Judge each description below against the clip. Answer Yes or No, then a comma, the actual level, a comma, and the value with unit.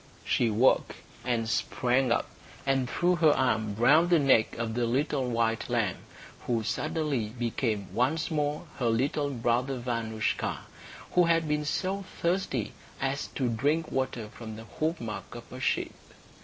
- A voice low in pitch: Yes, low, 125 Hz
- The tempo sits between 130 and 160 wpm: Yes, average, 150 wpm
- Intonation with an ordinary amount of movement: Yes, average, 4.6 semitones